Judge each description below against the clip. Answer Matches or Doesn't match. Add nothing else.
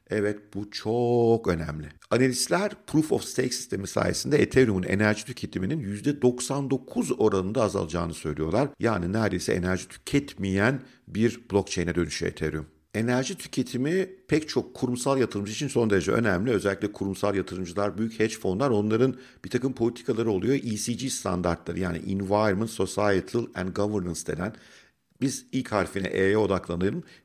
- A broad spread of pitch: Doesn't match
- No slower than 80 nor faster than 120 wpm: Doesn't match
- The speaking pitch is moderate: Doesn't match